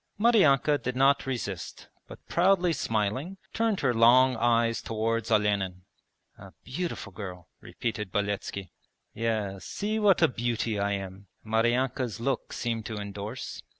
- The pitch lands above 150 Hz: No, low, 115 Hz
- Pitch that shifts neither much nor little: Yes, average, 4.5 semitones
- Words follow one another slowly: Yes, slow, 130 wpm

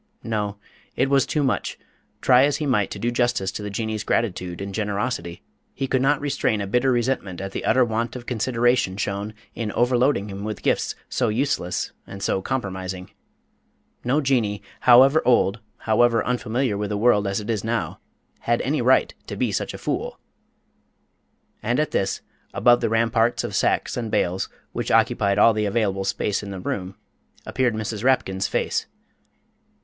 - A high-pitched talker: No, low, 110 Hz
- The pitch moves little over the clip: No, average, 3.7 semitones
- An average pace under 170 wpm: No, average, 175 wpm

